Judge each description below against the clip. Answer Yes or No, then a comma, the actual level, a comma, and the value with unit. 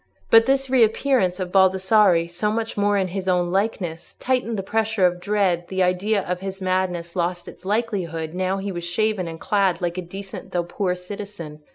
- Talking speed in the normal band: Yes, average, 190 wpm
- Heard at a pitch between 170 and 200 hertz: Yes, high, 190 Hz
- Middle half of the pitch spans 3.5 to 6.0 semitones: No, average, 2.9 semitones